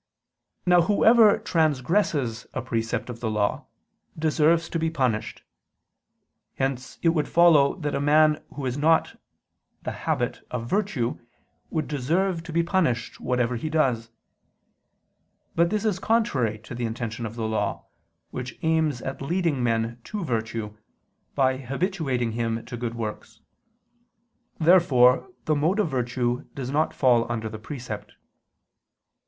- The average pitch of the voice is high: No, low, 135 Hz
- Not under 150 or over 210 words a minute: No, average, 140 wpm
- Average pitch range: No, wide, 5.7 semitones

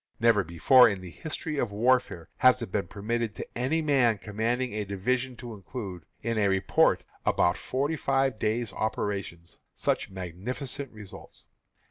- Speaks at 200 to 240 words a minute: No, average, 155 wpm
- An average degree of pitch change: Yes, average, 4.4 semitones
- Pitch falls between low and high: No, low, 110 Hz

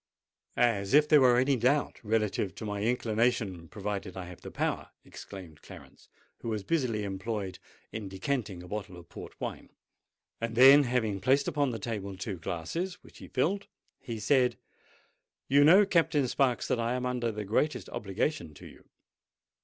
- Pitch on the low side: Yes, low, 115 Hz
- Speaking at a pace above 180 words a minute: No, average, 165 wpm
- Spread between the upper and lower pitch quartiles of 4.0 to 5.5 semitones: Yes, average, 5.1 semitones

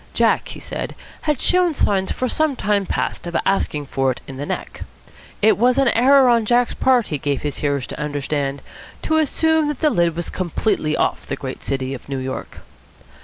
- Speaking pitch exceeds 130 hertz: Yes, high, 190 Hz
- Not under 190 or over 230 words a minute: Yes, average, 200 wpm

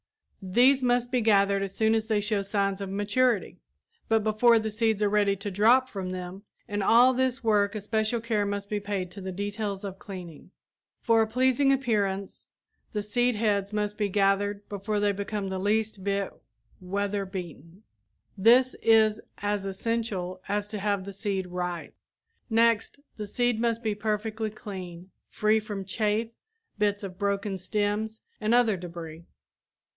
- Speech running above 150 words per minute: Yes, average, 160 wpm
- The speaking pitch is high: Yes, high, 205 Hz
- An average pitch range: No, narrow, 2.1 semitones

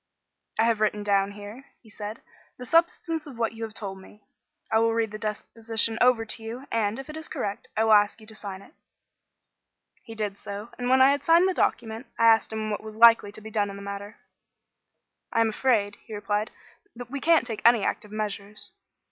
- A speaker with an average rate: No, fast, 215 wpm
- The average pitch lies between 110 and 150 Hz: No, high, 220 Hz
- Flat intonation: Yes, narrow, 2.2 semitones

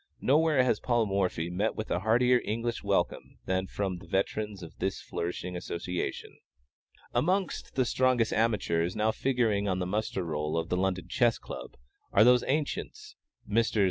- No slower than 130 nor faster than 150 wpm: No, average, 160 wpm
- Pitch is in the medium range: No, low, 105 Hz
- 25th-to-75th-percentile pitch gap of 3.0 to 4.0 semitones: No, average, 5.1 semitones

